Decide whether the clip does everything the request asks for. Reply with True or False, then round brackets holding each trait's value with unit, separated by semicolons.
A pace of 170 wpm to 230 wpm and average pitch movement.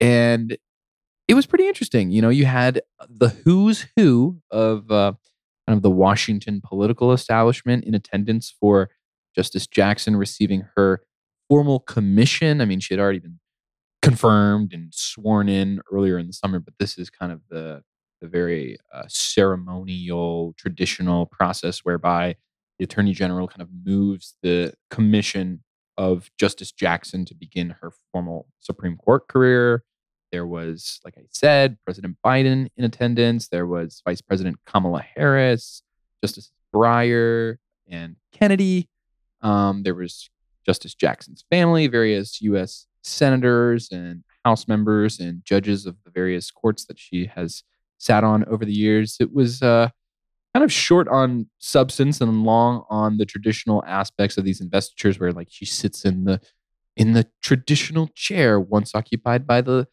False (150 wpm; 4.5 semitones)